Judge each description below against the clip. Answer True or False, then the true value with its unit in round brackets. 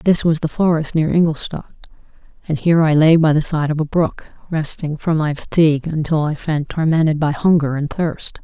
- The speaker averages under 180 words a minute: False (200 wpm)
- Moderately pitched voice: True (155 Hz)